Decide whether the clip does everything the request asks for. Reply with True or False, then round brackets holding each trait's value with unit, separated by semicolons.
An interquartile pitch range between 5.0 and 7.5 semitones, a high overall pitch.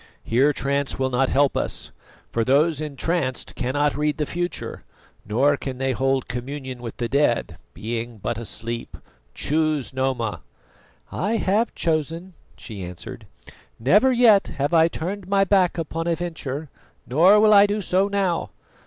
False (5.3 semitones; 145 Hz)